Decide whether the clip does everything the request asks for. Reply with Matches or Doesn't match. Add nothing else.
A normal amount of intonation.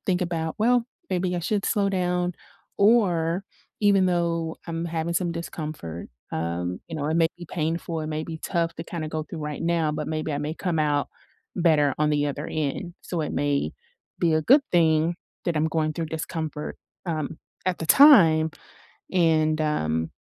Doesn't match